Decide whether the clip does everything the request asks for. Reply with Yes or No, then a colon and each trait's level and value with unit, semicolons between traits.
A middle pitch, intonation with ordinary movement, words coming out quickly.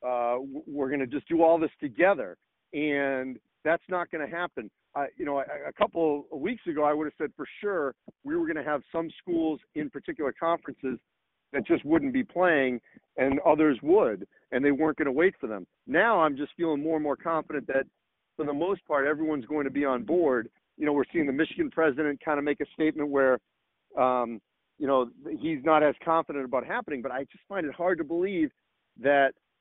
Yes: medium, 150 Hz; average, 3.4 semitones; fast, 215 wpm